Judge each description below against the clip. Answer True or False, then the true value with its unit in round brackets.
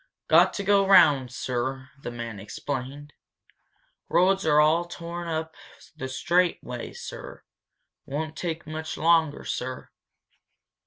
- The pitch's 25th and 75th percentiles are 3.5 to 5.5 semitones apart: True (4.4 semitones)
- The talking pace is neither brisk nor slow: False (120 wpm)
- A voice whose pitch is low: False (155 Hz)